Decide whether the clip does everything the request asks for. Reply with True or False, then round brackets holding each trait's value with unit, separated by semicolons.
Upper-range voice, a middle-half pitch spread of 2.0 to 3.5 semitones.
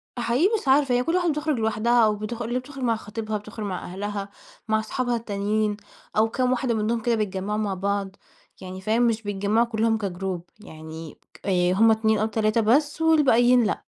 True (220 Hz; 3.0 semitones)